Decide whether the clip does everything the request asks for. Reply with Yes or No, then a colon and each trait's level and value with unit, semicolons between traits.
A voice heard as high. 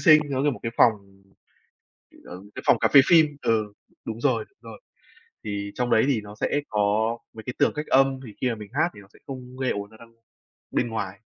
No: low, 115 Hz